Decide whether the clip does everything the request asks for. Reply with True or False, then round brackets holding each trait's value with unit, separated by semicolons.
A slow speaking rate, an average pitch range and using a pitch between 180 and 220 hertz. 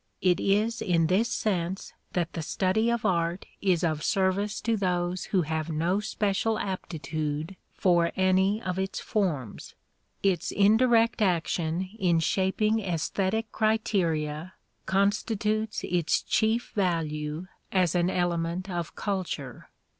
True (125 wpm; 3.5 semitones; 185 Hz)